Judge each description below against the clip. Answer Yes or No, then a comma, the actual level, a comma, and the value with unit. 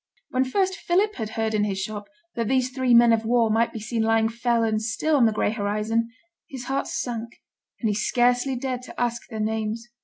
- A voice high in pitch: Yes, high, 230 Hz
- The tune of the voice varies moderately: No, narrow, 2.3 semitones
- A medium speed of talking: No, fast, 215 wpm